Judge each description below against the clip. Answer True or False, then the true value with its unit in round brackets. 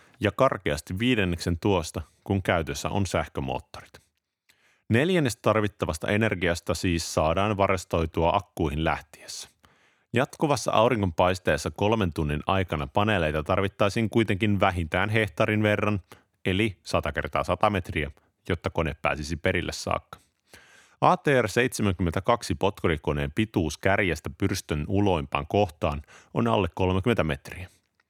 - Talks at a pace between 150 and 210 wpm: False (105 wpm)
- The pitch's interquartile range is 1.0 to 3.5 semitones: False (4.0 semitones)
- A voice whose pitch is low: True (95 Hz)